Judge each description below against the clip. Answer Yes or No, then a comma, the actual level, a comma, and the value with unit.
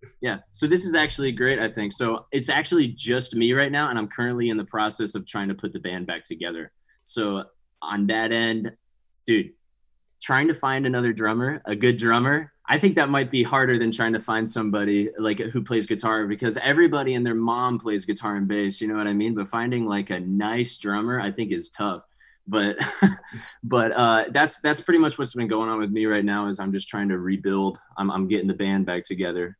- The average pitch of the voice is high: No, low, 110 Hz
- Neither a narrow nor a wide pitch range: Yes, average, 3.4 semitones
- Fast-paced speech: Yes, fast, 220 wpm